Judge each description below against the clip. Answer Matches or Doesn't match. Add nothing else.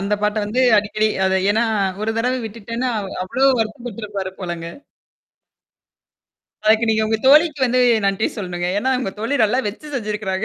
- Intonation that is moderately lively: Matches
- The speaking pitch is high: Matches